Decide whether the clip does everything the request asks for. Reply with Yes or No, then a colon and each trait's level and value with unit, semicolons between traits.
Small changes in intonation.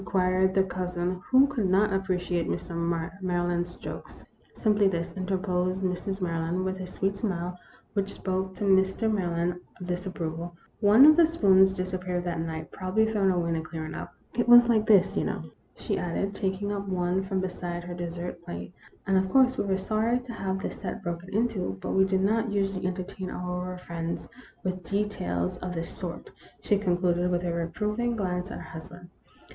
Yes: narrow, 2.1 semitones